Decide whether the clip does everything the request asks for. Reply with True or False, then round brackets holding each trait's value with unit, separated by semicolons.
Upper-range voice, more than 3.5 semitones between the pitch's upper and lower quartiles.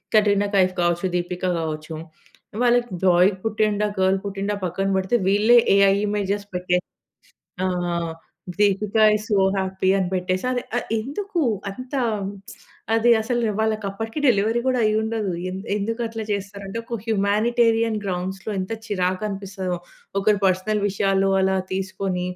False (200 Hz; 2.8 semitones)